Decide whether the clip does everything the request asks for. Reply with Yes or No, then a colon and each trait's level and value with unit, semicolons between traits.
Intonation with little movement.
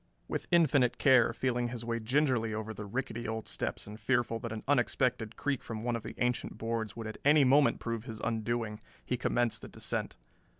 Yes: narrow, 2.3 semitones